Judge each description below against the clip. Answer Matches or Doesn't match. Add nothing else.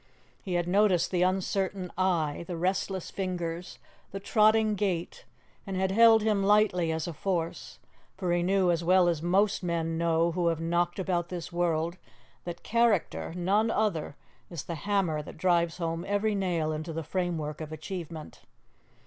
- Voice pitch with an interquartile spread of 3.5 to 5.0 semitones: Doesn't match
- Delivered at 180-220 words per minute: Doesn't match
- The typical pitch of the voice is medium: Matches